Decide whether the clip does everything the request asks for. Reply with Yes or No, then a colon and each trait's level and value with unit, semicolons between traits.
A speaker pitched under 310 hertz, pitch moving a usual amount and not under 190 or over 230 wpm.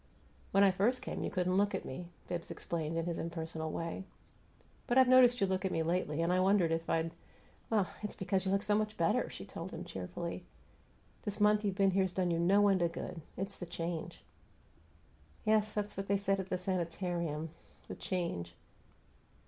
Yes: medium, 185 Hz; average, 3.0 semitones; average, 195 wpm